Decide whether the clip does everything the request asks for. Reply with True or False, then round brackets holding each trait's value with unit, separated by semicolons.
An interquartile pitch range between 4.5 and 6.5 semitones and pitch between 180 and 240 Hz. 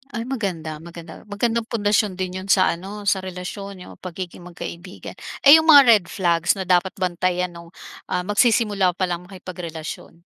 False (2.7 semitones; 185 Hz)